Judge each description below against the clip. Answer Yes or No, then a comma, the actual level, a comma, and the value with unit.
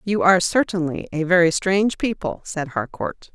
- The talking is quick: No, average, 160 wpm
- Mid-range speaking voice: Yes, medium, 180 Hz